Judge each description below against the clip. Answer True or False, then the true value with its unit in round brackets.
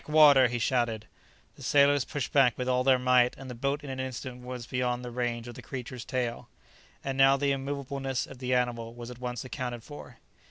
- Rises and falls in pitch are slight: True (1.8 semitones)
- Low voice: True (125 Hz)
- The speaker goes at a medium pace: False (210 wpm)